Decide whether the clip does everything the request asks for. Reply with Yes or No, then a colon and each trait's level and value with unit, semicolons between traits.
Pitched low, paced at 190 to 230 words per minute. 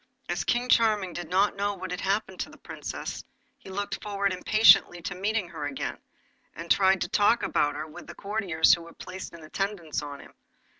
No: high, 190 Hz; fast, 205 wpm